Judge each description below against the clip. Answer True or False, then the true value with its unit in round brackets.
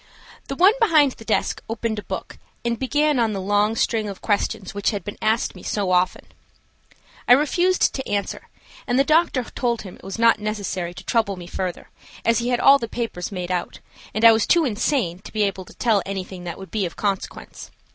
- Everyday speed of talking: False (215 wpm)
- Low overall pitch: False (215 Hz)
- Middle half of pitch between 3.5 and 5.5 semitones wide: True (4.1 semitones)